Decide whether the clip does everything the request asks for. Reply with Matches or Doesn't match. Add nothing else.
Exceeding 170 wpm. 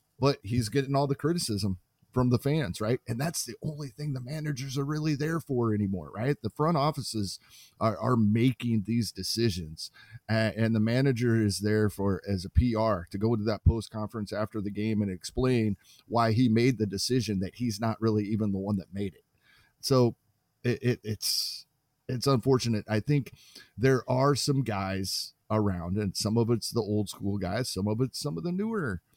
Matches